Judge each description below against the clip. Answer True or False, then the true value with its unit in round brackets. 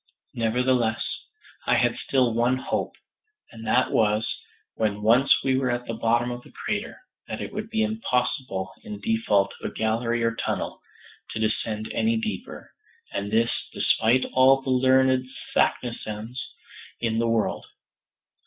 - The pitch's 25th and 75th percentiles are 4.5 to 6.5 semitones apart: False (2.8 semitones)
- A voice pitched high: False (120 Hz)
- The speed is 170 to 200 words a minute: False (145 wpm)